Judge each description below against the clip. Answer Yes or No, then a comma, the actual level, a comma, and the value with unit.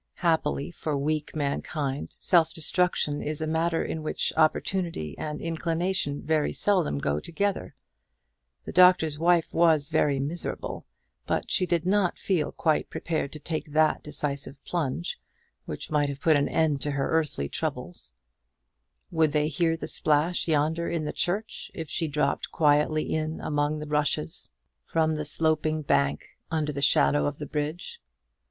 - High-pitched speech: No, medium, 155 Hz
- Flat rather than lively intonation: Yes, narrow, 2.1 semitones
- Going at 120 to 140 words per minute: No, average, 155 wpm